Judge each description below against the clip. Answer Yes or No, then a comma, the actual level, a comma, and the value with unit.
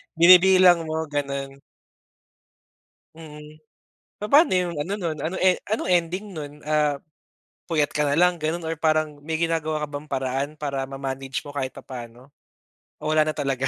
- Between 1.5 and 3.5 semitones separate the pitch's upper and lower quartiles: Yes, average, 3.2 semitones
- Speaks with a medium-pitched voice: Yes, medium, 155 Hz